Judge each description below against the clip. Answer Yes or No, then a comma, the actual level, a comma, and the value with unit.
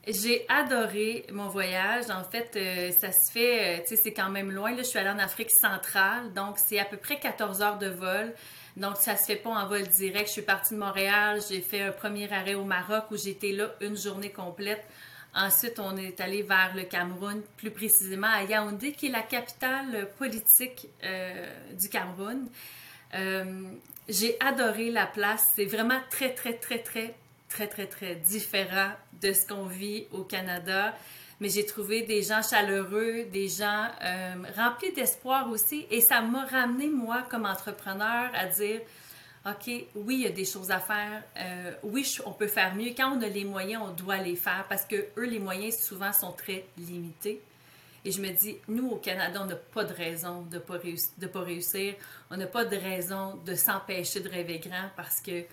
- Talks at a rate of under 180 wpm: No, average, 195 wpm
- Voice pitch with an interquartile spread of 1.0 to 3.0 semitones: Yes, average, 2.7 semitones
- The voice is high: Yes, high, 205 Hz